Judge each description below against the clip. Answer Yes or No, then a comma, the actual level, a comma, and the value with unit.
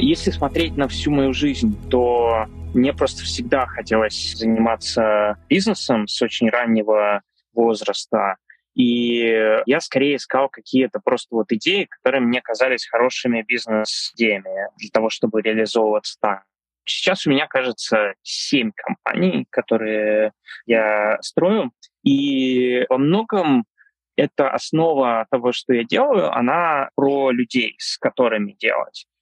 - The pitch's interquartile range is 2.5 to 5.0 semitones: Yes, average, 4.0 semitones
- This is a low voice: Yes, low, 120 Hz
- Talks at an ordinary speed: Yes, average, 120 wpm